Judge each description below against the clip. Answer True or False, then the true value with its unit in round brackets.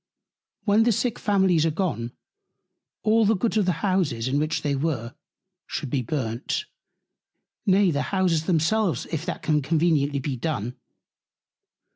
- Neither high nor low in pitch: True (160 Hz)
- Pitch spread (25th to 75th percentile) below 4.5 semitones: False (5.3 semitones)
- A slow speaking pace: False (145 wpm)